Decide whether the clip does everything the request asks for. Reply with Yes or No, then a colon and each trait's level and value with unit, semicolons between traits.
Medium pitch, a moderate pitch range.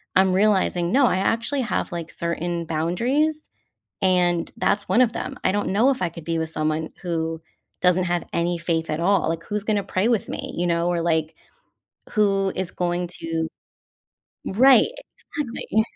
Yes: medium, 180 Hz; average, 3.9 semitones